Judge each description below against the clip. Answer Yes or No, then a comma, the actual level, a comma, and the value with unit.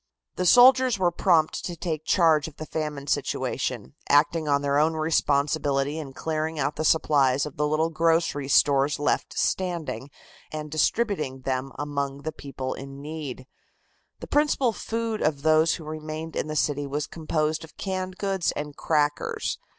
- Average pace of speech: Yes, average, 160 wpm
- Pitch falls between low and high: Yes, medium, 155 Hz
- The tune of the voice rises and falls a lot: No, narrow, 2.5 semitones